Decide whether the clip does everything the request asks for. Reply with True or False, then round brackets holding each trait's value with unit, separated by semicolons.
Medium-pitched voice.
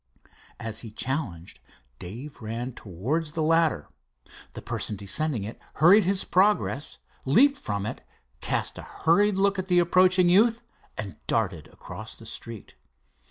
True (155 Hz)